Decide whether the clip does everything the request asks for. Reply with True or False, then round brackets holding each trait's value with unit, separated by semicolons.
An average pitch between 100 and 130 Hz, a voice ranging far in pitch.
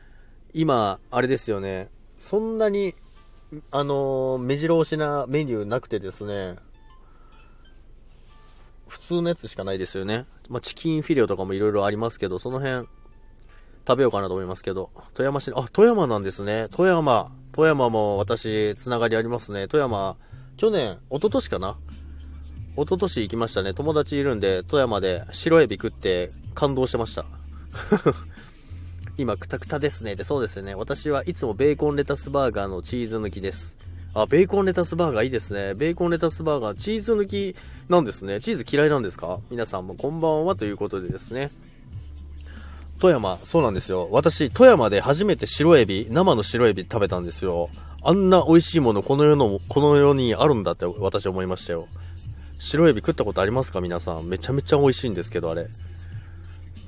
True (110 Hz; 7.5 semitones)